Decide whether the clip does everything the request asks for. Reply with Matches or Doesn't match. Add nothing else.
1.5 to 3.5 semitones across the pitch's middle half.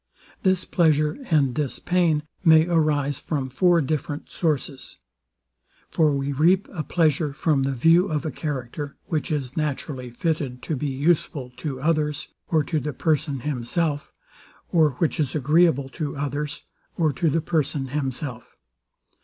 Matches